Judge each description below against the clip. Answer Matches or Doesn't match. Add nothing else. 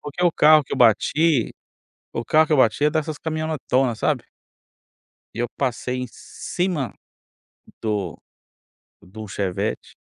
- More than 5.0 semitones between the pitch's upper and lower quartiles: Matches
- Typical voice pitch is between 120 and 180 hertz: Matches